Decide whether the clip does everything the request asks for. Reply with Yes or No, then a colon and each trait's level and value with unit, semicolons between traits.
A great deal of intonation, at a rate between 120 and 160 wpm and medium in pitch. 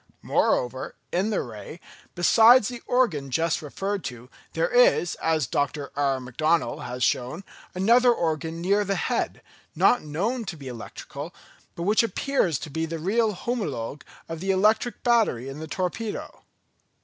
Yes: wide, 7.1 semitones; average, 150 wpm; medium, 170 Hz